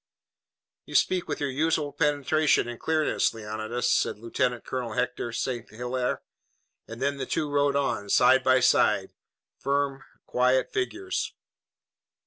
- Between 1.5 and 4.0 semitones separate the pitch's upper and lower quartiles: Yes, average, 3.1 semitones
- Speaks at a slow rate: Yes, slow, 130 wpm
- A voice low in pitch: Yes, low, 130 Hz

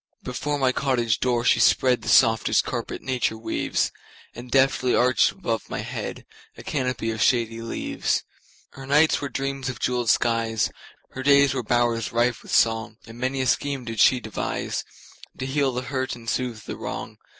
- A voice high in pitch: No, low, 125 Hz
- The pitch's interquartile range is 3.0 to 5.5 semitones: No, narrow, 2.5 semitones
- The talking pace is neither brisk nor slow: Yes, average, 150 wpm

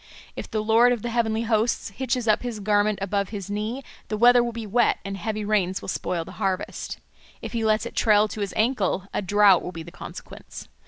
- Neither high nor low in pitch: No, high, 215 Hz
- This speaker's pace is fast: Yes, fast, 220 wpm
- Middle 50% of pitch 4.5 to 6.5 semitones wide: No, narrow, 2.6 semitones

